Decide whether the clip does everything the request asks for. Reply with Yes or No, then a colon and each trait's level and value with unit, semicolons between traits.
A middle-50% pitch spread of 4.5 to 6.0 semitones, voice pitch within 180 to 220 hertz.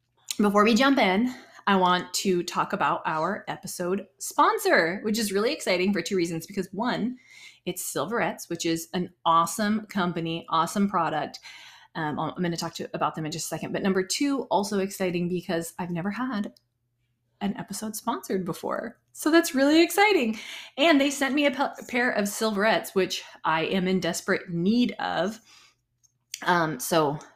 Yes: average, 5.3 semitones; high, 190 Hz